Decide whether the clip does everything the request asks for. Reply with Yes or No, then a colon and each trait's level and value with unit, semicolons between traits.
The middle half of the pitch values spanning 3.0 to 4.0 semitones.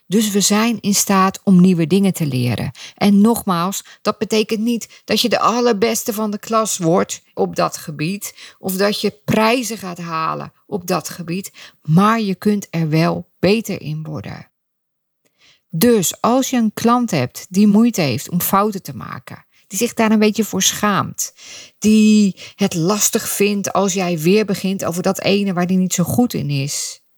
Yes: average, 3.6 semitones